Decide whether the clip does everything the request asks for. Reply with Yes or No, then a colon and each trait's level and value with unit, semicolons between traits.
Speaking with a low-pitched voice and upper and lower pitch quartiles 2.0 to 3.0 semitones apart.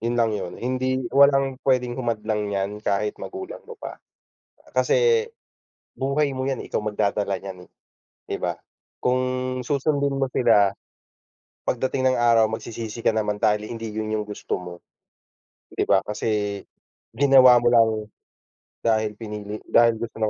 No: low, 115 Hz; average, 3.6 semitones